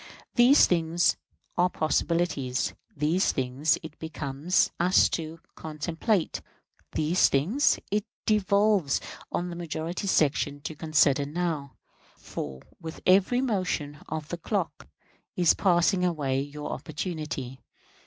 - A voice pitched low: No, medium, 160 Hz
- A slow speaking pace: Yes, slow, 115 wpm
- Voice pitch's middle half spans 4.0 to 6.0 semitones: No, average, 3.6 semitones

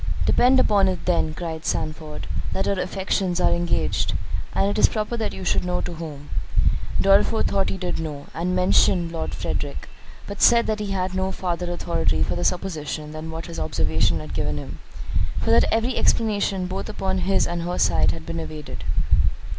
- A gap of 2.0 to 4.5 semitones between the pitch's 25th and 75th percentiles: Yes, average, 3.9 semitones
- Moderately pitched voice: Yes, medium, 180 Hz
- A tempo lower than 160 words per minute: No, average, 185 wpm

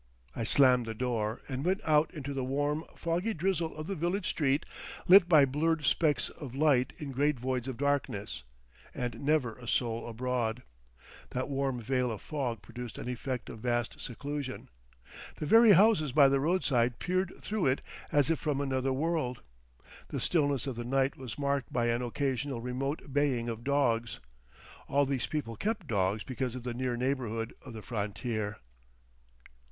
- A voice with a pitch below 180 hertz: Yes, low, 135 Hz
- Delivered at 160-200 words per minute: Yes, average, 170 wpm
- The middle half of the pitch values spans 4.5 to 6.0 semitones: No, average, 3.6 semitones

